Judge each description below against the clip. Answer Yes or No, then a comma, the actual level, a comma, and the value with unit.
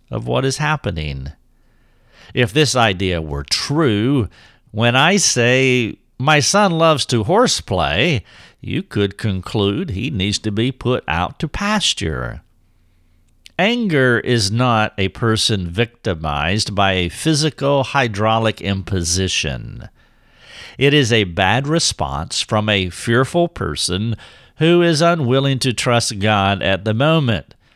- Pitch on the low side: Yes, low, 110 Hz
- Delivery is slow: Yes, slow, 125 wpm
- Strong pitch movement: Yes, wide, 5.9 semitones